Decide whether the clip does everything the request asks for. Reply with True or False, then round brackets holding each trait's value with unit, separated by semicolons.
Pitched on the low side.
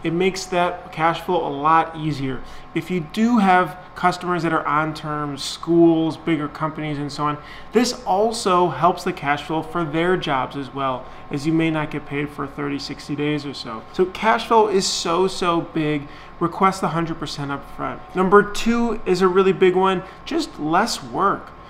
False (165 Hz)